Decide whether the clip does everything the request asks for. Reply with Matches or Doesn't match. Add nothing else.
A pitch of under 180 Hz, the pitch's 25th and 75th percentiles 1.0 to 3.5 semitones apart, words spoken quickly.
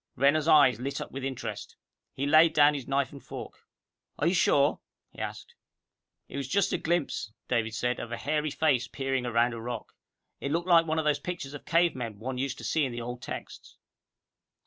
Doesn't match